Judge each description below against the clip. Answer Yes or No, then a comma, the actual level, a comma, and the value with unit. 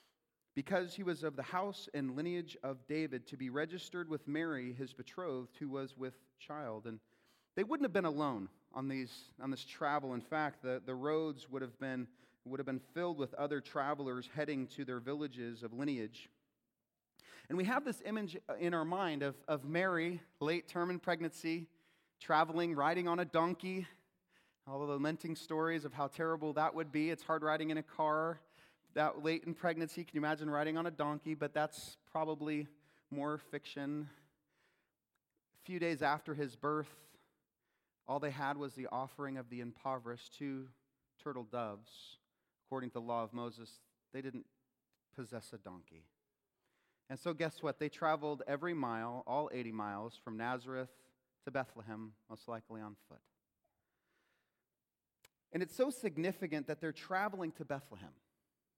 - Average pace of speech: Yes, average, 165 wpm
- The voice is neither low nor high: Yes, medium, 145 Hz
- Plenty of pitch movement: No, average, 3.9 semitones